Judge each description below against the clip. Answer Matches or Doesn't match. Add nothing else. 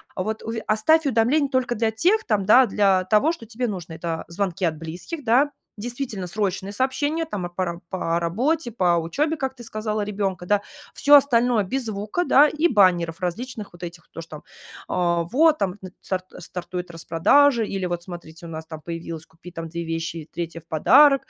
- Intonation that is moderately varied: Doesn't match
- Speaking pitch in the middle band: Doesn't match